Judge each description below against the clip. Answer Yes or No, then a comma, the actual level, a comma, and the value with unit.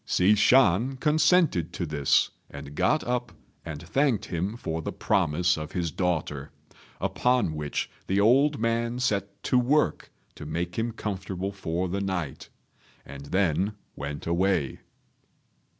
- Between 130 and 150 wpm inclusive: Yes, slow, 135 wpm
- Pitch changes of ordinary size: No, wide, 6.5 semitones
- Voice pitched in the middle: No, very low, 95 Hz